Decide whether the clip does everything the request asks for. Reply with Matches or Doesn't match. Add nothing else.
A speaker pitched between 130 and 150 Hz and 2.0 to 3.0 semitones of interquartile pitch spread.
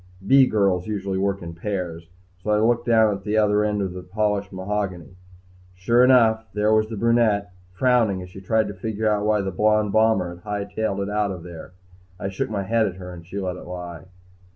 Doesn't match